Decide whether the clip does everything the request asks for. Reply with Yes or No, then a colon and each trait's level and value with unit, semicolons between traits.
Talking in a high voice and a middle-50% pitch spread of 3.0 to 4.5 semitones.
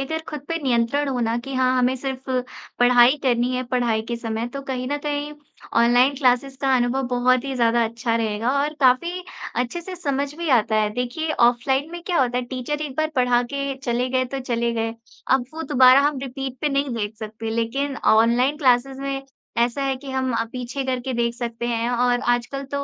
No: very high, 255 Hz; narrow, 2.4 semitones